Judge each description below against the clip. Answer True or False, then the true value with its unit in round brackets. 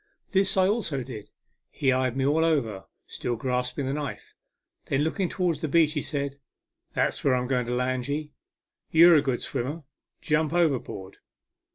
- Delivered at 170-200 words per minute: True (180 wpm)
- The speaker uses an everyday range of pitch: True (4.1 semitones)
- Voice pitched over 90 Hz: True (140 Hz)